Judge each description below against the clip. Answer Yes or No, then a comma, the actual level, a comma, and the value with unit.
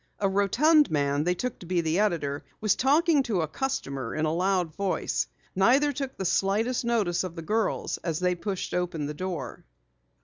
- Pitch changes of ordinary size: No, wide, 5.8 semitones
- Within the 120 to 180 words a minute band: No, average, 190 wpm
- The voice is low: No, medium, 185 Hz